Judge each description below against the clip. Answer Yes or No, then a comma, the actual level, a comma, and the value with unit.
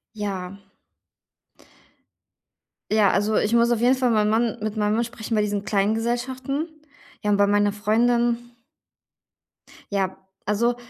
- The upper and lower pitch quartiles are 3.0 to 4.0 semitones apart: No, narrow, 2.6 semitones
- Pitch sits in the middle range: No, high, 220 Hz